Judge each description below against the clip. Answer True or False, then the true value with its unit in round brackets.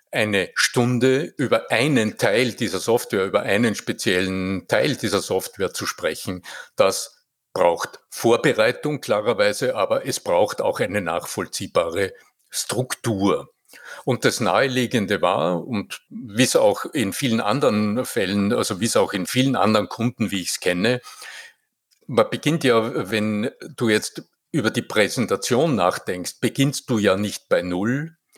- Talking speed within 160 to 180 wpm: False (140 wpm)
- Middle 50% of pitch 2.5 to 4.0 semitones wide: False (4.7 semitones)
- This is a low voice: True (120 Hz)